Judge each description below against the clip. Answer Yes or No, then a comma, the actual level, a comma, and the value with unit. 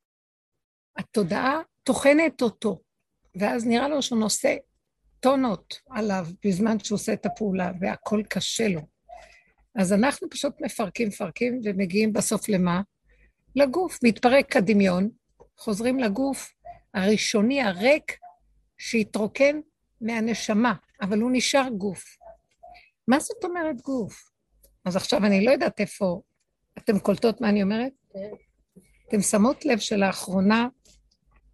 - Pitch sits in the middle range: No, high, 225 Hz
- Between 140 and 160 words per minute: No, average, 110 wpm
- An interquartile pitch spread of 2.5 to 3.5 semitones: No, average, 4.8 semitones